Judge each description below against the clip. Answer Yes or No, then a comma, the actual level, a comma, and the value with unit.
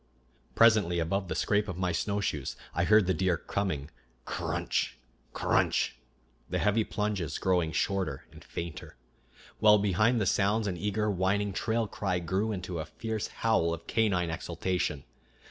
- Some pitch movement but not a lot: Yes, average, 3.4 semitones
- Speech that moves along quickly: No, average, 165 wpm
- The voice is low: Yes, very low, 95 Hz